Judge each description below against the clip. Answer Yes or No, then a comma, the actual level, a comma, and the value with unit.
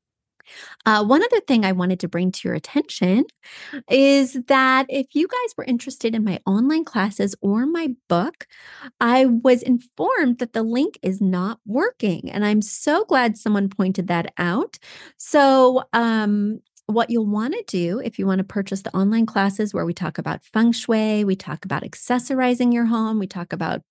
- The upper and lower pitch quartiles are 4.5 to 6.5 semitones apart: Yes, average, 4.8 semitones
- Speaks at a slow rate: No, average, 180 wpm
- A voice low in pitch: No, high, 225 Hz